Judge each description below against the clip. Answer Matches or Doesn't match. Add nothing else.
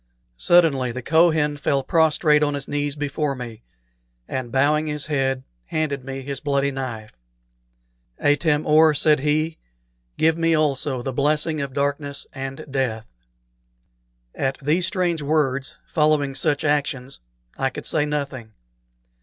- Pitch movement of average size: Doesn't match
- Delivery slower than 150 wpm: Matches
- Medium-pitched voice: Matches